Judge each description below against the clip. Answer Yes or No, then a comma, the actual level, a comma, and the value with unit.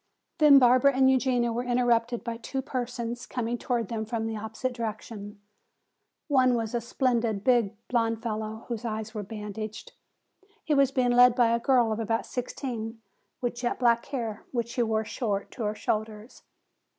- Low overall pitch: No, high, 235 Hz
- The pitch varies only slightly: Yes, narrow, 2.1 semitones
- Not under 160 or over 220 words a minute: Yes, average, 170 wpm